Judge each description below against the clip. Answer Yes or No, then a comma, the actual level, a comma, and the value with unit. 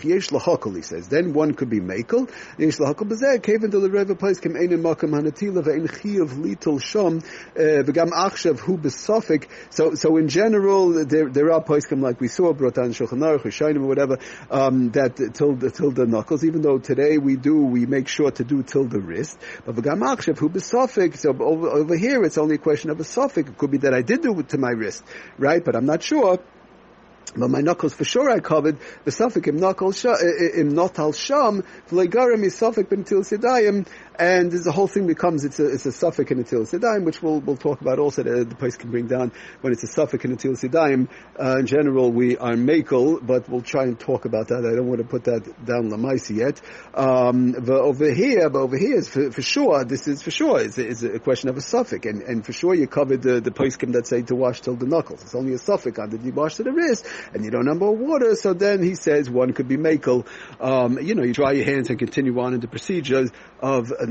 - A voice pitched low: No, medium, 150 Hz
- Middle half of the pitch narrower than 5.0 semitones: No, average, 5.3 semitones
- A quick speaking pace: Yes, fast, 220 wpm